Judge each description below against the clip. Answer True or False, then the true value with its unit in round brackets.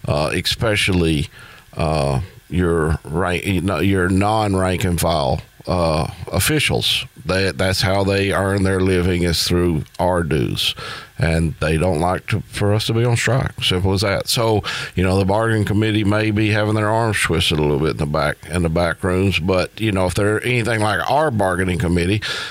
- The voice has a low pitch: True (95 Hz)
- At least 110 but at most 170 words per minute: False (180 wpm)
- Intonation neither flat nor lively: True (3.3 semitones)